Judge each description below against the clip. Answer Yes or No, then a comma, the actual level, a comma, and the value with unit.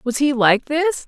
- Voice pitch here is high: Yes, very high, 275 Hz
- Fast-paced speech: Yes, fast, 225 wpm